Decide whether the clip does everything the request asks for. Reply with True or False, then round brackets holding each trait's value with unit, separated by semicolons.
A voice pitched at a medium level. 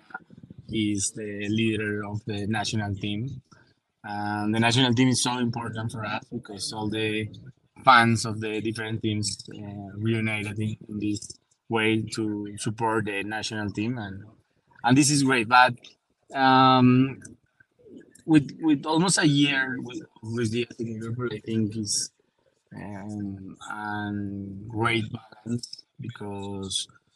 False (110 Hz)